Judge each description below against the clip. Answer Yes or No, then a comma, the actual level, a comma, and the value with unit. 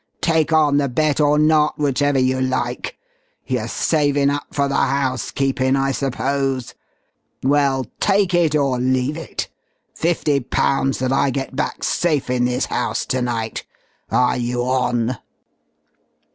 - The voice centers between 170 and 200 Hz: No, low, 135 Hz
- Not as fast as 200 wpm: Yes, average, 140 wpm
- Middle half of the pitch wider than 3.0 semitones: No, narrow, 2.4 semitones